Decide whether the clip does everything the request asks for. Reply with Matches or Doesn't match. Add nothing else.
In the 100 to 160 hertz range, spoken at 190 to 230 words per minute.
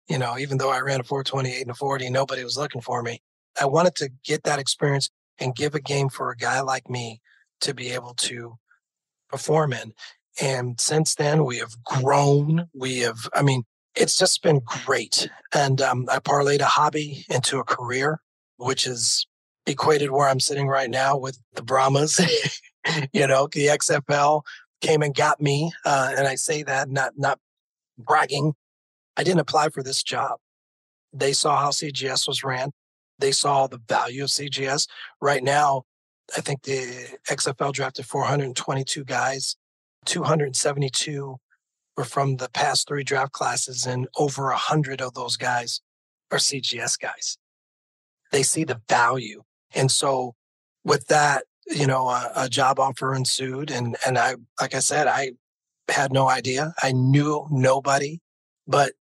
Doesn't match